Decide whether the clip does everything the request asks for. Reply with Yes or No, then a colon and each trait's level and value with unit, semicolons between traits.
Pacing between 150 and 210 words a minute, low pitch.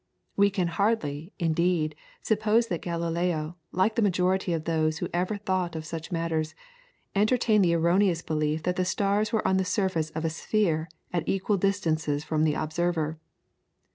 No: average, 165 wpm; medium, 175 Hz